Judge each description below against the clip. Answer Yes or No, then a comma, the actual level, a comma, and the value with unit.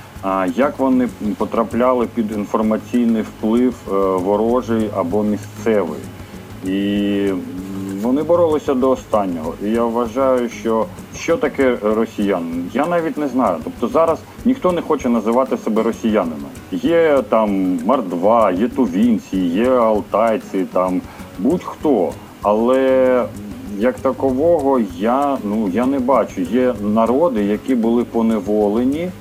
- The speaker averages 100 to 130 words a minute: Yes, average, 115 wpm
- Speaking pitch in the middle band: No, low, 115 Hz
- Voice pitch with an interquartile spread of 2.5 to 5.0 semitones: Yes, average, 4.3 semitones